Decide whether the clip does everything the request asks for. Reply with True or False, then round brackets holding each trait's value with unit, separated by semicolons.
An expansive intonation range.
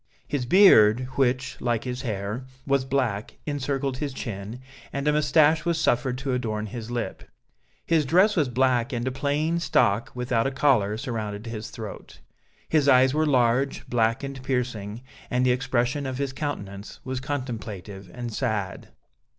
False (3.6 semitones)